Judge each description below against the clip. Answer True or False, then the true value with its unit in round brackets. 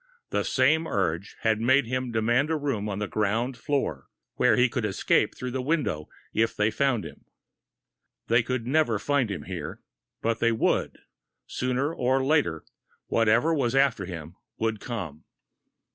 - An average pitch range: True (4.0 semitones)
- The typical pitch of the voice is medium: False (120 Hz)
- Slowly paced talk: False (160 wpm)